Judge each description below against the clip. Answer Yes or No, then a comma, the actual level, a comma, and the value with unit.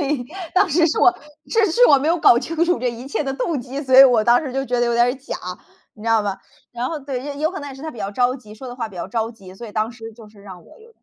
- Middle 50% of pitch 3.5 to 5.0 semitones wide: Yes, average, 4.1 semitones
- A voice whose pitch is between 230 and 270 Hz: Yes, very high, 250 Hz